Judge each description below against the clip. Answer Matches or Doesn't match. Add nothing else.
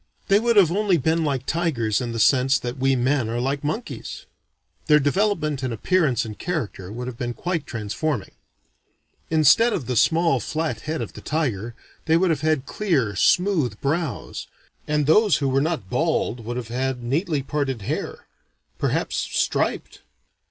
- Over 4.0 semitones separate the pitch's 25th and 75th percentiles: Matches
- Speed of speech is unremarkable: Matches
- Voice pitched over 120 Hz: Matches